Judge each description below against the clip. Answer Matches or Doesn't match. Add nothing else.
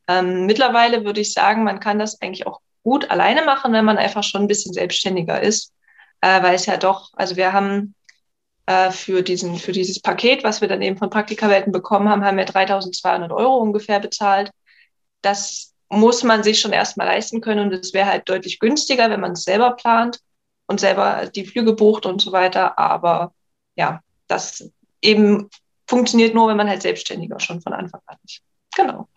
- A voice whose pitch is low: Doesn't match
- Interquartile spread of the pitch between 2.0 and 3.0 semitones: Matches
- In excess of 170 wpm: Matches